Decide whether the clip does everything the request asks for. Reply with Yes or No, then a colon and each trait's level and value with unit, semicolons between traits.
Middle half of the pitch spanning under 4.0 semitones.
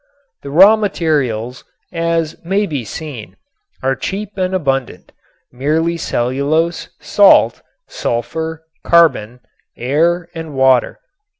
No: average, 4.3 semitones